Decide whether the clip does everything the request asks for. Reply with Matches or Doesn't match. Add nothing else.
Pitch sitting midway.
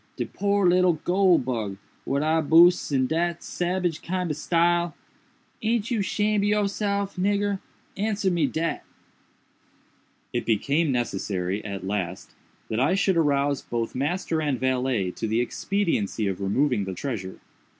Matches